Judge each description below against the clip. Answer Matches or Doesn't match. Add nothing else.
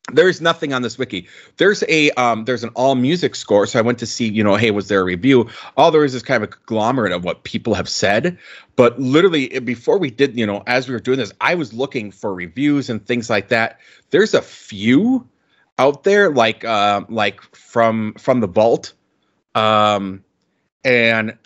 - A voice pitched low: Matches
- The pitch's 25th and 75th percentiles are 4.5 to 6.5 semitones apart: Doesn't match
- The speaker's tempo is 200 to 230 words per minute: Matches